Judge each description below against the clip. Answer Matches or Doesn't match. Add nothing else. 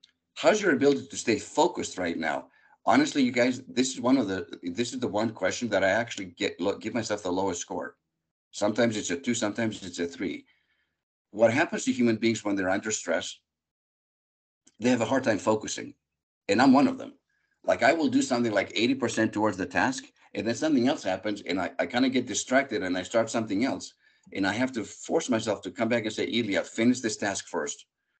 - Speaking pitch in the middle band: Doesn't match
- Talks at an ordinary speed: Doesn't match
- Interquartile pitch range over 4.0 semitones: Matches